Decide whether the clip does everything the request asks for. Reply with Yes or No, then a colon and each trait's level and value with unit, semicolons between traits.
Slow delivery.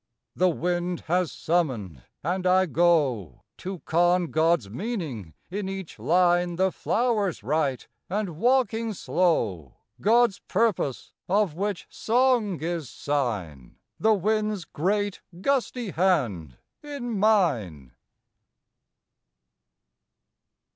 Yes: slow, 100 wpm